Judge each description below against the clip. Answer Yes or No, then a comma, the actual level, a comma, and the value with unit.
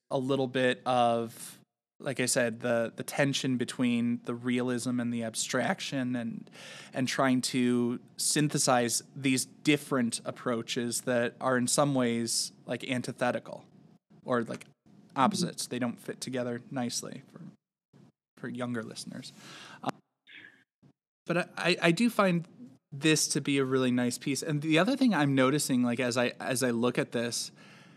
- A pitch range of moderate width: Yes, average, 3.6 semitones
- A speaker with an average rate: Yes, average, 150 wpm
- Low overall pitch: Yes, low, 130 Hz